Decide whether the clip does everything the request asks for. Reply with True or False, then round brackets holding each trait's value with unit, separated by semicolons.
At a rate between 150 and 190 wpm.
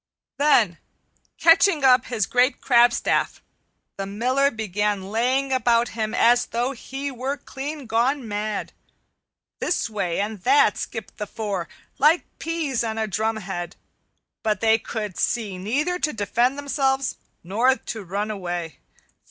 False (135 wpm)